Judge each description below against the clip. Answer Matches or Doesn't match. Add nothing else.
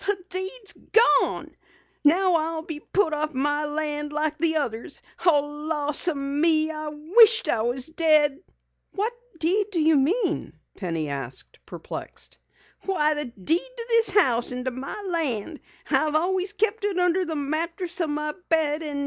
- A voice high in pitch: Matches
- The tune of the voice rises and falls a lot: Doesn't match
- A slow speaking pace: Doesn't match